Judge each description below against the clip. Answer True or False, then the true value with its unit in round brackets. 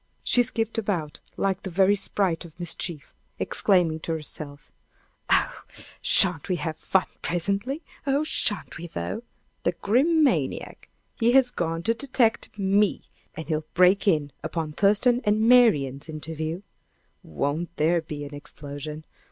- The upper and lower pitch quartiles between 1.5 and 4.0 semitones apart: False (5.2 semitones)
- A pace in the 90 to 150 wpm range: True (140 wpm)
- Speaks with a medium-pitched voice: True (175 Hz)